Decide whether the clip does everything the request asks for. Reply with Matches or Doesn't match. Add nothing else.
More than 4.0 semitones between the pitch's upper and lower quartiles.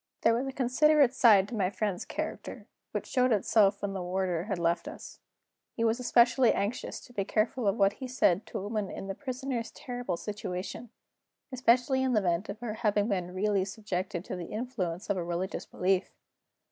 Matches